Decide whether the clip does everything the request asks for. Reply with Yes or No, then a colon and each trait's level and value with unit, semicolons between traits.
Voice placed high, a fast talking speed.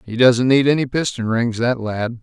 No: low, 120 Hz; fast, 215 wpm